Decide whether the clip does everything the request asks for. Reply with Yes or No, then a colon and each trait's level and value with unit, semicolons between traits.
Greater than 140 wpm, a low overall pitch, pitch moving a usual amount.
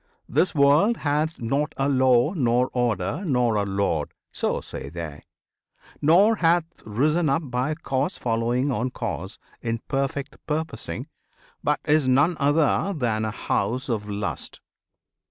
No: slow, 135 wpm; low, 130 Hz; average, 4.9 semitones